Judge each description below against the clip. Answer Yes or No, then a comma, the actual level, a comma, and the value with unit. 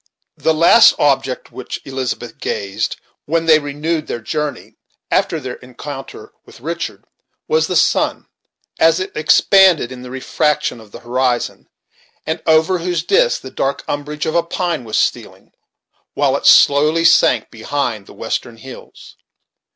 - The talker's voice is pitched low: No, medium, 145 Hz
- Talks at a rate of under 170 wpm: Yes, average, 150 wpm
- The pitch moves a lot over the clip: No, average, 4.3 semitones